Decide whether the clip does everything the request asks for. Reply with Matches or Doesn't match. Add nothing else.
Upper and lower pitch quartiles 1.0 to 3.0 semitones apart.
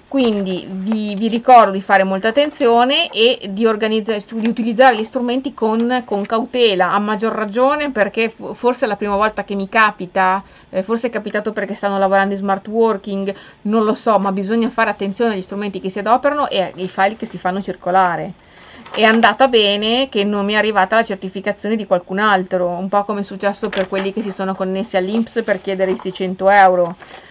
Matches